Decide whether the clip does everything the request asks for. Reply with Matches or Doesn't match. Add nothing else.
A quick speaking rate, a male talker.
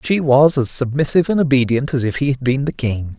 Matches